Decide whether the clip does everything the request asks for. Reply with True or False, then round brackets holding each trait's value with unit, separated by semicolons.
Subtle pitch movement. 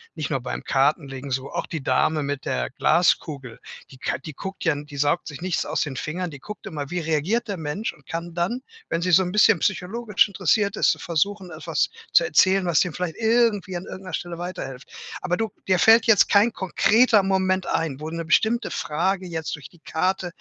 False (4.4 semitones)